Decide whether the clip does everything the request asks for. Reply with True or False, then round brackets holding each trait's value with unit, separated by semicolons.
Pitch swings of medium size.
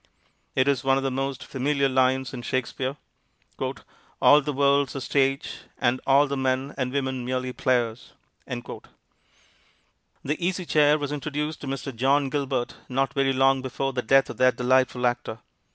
False (1.5 semitones)